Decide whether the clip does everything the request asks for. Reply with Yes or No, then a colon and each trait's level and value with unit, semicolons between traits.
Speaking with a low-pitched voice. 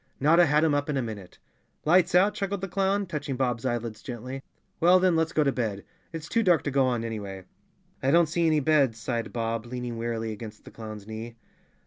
Yes: low, 130 Hz